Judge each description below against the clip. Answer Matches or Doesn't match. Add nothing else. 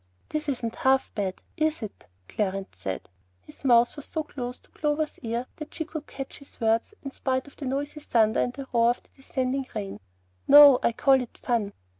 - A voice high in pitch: Matches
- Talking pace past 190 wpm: Matches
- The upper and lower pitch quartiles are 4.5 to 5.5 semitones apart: Doesn't match